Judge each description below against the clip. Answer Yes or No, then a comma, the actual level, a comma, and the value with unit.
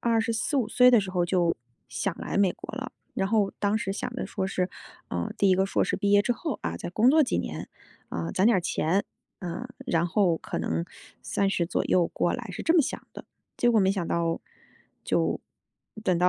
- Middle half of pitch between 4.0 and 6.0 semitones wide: Yes, average, 4.4 semitones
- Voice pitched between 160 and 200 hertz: Yes, high, 195 Hz